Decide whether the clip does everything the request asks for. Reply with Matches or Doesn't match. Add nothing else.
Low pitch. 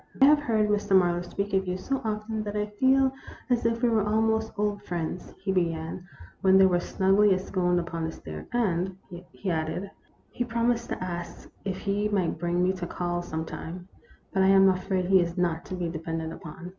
Doesn't match